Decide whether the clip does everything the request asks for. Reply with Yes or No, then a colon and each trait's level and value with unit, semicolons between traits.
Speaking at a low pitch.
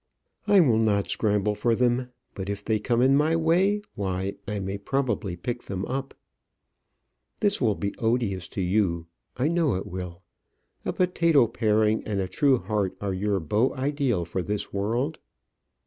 Yes: low, 110 Hz